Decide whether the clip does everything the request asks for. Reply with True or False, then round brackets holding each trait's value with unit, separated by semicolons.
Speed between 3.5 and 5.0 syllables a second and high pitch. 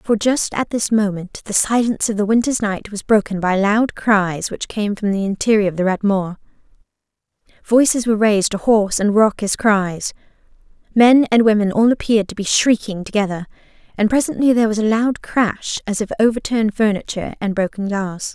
False (5.4 syllables/s; 210 Hz)